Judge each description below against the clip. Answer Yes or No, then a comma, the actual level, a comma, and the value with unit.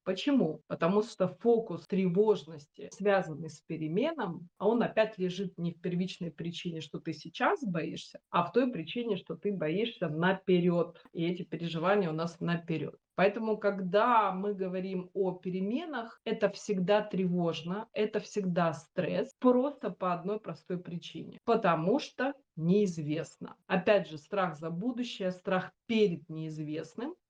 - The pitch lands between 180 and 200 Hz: Yes, medium, 185 Hz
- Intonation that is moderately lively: Yes, average, 3.7 semitones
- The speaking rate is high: No, average, 135 wpm